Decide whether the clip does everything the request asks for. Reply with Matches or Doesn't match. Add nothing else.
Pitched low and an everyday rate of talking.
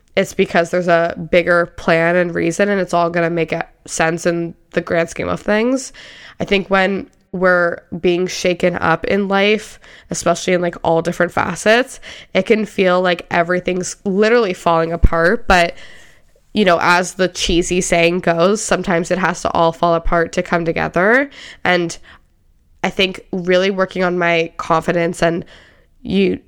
Doesn't match